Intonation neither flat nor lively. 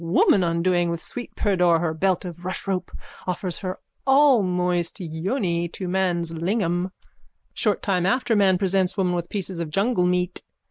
No: narrow, 2.1 semitones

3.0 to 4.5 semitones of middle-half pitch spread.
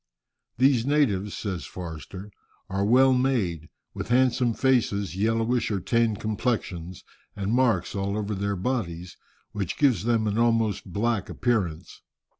Yes: average, 3.9 semitones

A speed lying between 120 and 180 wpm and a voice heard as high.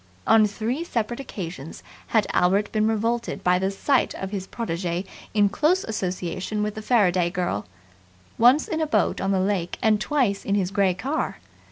Yes: average, 175 wpm; high, 205 Hz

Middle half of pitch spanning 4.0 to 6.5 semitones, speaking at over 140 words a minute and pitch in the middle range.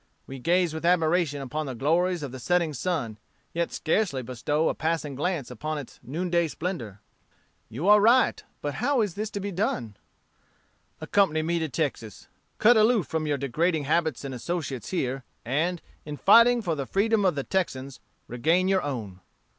Yes: average, 5.0 semitones; average, 170 wpm; medium, 160 Hz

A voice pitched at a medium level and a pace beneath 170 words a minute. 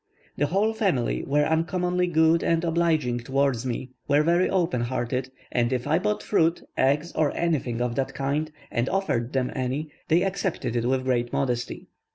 No: medium, 145 Hz; average, 175 wpm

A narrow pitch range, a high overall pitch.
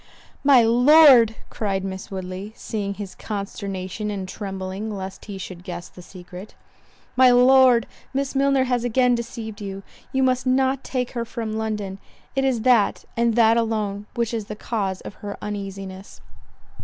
No: average, 3.9 semitones; high, 220 Hz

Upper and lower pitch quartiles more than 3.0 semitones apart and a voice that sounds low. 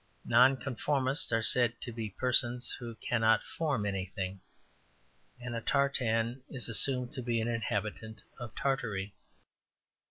No: narrow, 2.5 semitones; low, 120 Hz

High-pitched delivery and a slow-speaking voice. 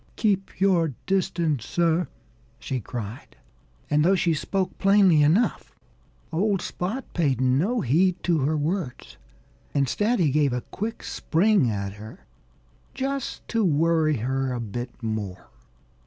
No: medium, 160 Hz; slow, 130 wpm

